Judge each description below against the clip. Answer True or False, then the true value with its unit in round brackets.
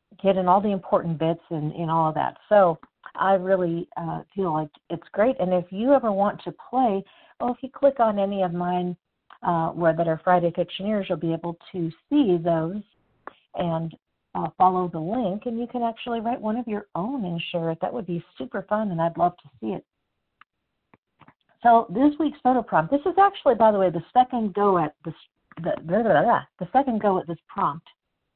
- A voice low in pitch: False (185 Hz)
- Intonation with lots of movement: False (5.0 semitones)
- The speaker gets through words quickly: True (215 wpm)